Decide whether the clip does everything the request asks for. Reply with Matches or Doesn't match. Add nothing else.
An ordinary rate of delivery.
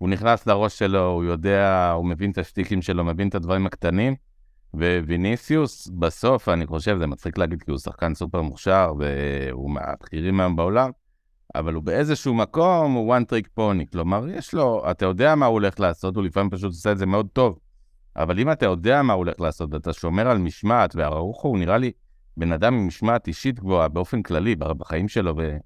Doesn't match